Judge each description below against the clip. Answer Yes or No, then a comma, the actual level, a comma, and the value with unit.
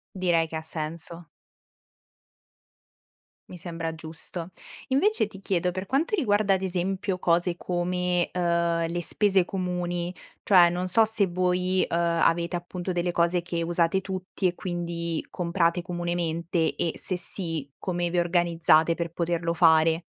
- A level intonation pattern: Yes, narrow, 1.5 semitones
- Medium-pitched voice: Yes, medium, 175 Hz